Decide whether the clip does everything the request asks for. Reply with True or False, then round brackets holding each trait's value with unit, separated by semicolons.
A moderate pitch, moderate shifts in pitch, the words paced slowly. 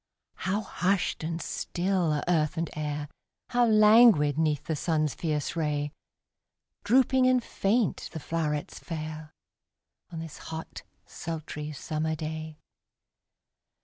True (160 Hz; 3.7 semitones; 115 wpm)